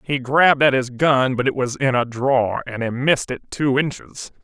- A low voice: Yes, low, 130 Hz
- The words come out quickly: Yes, fast, 230 wpm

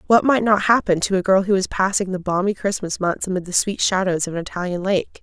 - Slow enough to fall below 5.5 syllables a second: No, 5.9 syllables/s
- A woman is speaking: Yes, female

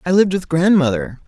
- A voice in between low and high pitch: Yes, medium, 160 Hz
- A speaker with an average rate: Yes, average, 190 wpm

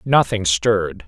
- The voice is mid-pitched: No, low, 100 Hz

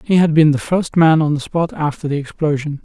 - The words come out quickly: Yes, fast, 255 wpm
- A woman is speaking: No, male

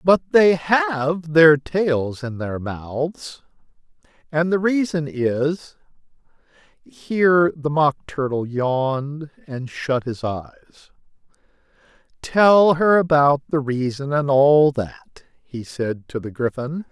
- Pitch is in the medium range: Yes, medium, 150 Hz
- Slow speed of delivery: Yes, slow, 115 wpm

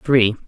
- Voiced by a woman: No, male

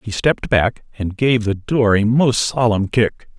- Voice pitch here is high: No, low, 115 Hz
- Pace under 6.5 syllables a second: Yes, 4.2 syllables/s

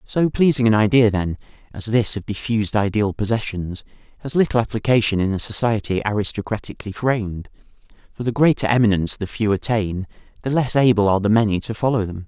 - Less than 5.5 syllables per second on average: No, 6.2 syllables/s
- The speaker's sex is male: Yes, male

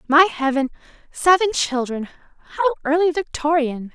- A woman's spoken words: Yes, female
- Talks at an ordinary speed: No, slow, 90 wpm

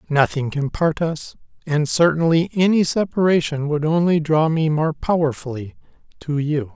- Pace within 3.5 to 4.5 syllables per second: No, 4.7 syllables/s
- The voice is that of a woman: No, male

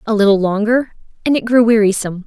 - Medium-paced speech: Yes, average, 185 wpm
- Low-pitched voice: No, high, 215 Hz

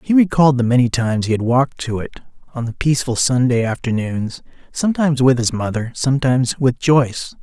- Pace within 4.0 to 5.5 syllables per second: No, 6.1 syllables/s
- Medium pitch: No, low, 130 Hz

